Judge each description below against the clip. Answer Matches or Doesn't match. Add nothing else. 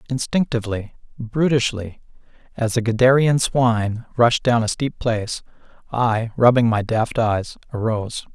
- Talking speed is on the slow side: Matches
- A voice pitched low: Matches